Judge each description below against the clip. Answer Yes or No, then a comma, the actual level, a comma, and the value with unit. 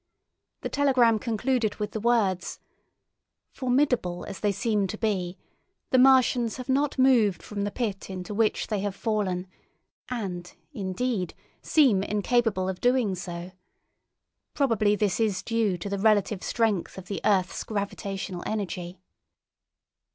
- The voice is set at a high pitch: Yes, high, 210 Hz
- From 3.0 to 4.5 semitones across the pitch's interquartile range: Yes, average, 3.9 semitones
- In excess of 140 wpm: No, slow, 135 wpm